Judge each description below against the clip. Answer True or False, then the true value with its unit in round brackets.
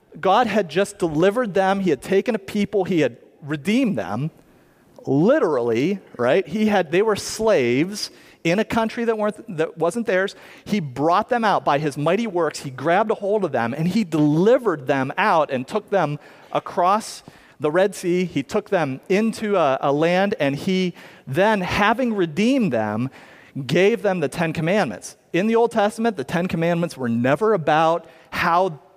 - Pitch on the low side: False (185 Hz)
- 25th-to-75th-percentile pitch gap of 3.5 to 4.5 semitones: False (5.1 semitones)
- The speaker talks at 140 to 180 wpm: True (175 wpm)